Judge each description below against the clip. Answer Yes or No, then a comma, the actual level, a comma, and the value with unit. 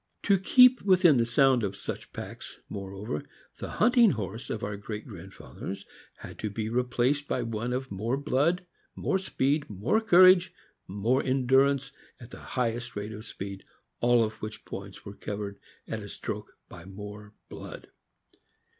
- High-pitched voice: No, low, 120 Hz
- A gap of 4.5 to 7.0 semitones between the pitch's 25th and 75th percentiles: Yes, average, 5.2 semitones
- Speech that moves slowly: No, average, 155 wpm